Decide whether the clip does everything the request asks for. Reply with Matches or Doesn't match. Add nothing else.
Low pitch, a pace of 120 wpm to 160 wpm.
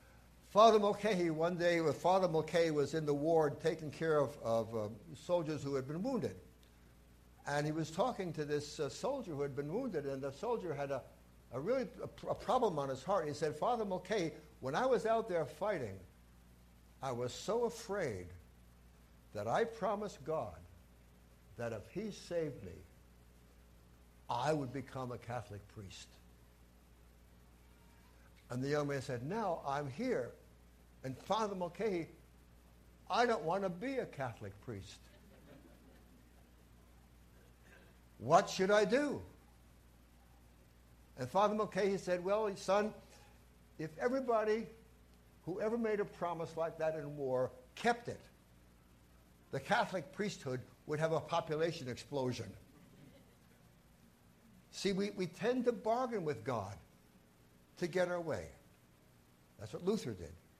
Matches